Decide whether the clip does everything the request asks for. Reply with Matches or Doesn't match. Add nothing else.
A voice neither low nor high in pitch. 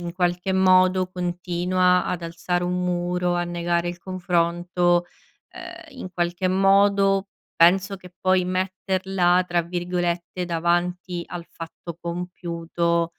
Matches